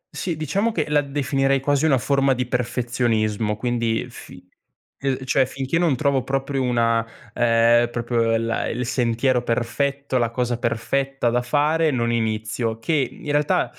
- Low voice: Yes, low, 125 Hz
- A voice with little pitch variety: No, average, 3.0 semitones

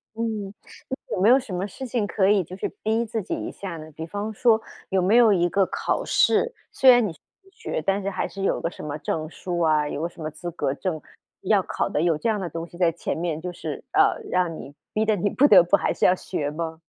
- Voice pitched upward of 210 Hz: No, medium, 185 Hz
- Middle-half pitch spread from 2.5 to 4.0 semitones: No, average, 4.4 semitones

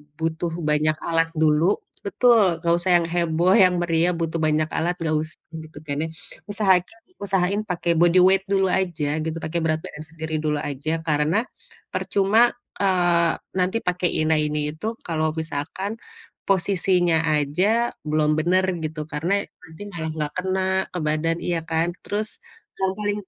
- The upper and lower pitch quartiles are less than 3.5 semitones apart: Yes, average, 3.1 semitones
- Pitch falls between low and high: Yes, medium, 165 Hz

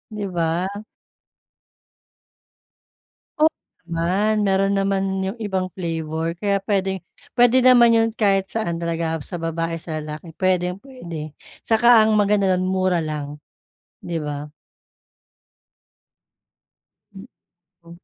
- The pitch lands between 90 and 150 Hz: No, medium, 185 Hz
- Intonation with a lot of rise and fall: No, average, 3.7 semitones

